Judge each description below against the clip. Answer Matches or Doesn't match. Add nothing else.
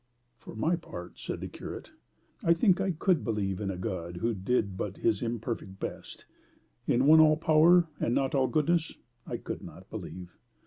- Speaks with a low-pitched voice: Matches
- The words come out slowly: Doesn't match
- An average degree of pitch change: Doesn't match